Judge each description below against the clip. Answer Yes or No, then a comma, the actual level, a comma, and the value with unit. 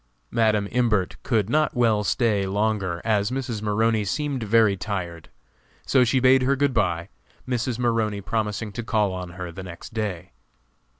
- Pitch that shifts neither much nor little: Yes, average, 3.4 semitones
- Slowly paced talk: No, average, 160 wpm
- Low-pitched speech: Yes, low, 110 Hz